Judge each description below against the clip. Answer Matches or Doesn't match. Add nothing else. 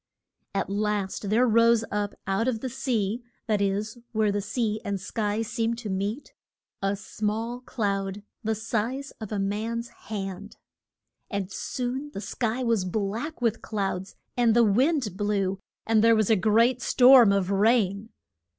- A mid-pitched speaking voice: Doesn't match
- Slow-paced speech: Doesn't match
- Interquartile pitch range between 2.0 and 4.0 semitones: Matches